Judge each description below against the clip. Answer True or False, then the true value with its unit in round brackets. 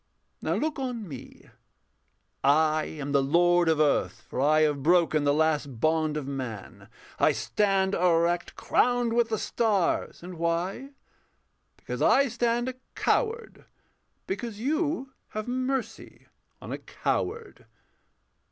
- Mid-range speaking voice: True (175 Hz)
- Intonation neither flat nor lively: False (7.7 semitones)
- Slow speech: True (130 wpm)